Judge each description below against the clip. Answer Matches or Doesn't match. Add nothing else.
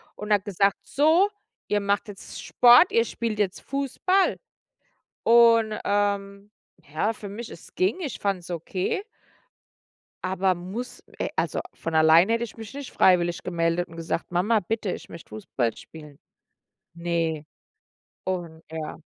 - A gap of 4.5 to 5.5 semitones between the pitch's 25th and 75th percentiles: Matches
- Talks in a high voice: Matches